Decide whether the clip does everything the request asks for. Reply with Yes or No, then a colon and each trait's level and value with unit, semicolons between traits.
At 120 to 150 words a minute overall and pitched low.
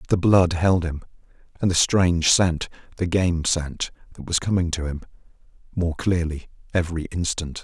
Yes: average, 140 wpm; very low, 85 Hz